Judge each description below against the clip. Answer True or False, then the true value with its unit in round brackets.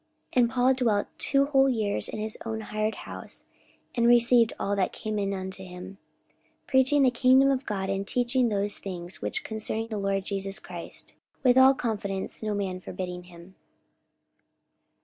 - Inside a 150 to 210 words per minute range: True (170 wpm)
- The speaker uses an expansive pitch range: False (4.2 semitones)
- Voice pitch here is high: True (215 Hz)